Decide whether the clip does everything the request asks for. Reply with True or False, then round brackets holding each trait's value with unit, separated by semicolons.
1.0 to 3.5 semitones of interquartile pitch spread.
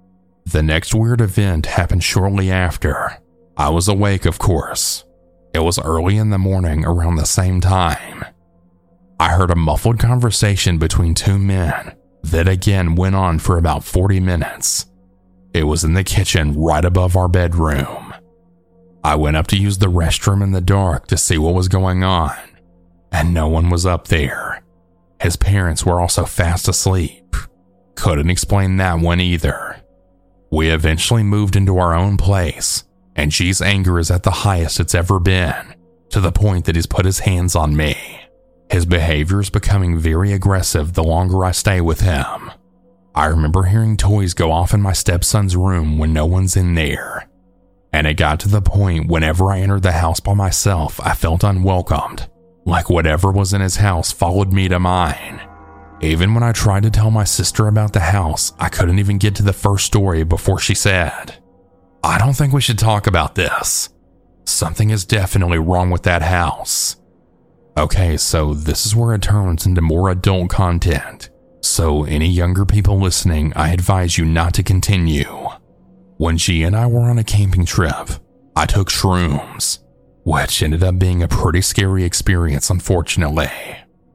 True (2.9 semitones)